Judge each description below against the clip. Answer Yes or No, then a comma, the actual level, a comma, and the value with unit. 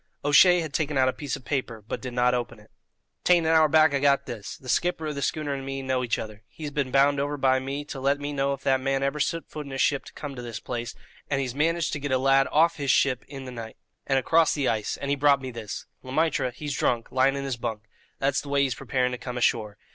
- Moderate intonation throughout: No, narrow, 2.3 semitones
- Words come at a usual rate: No, fast, 275 wpm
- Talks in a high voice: No, low, 135 Hz